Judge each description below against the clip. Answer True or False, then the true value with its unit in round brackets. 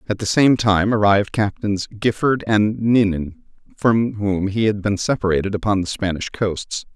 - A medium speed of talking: True (165 wpm)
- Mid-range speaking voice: False (105 Hz)